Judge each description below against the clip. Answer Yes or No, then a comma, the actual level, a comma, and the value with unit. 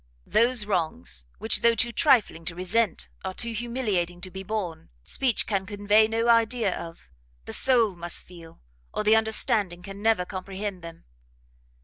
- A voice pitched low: No, high, 205 Hz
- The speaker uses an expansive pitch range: No, average, 4.2 semitones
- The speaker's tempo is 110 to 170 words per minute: Yes, average, 155 wpm